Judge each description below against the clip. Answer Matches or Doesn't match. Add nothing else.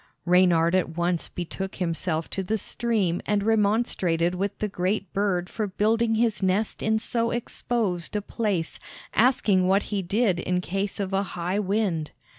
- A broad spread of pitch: Doesn't match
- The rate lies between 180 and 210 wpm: Doesn't match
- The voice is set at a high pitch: Matches